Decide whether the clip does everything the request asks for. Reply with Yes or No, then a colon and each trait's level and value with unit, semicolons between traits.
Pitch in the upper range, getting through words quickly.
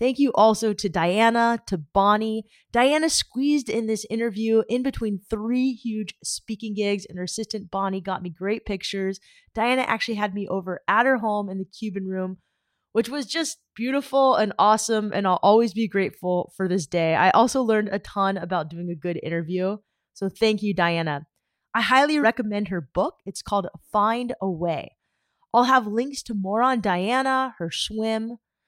No: high, 215 Hz; average, 180 wpm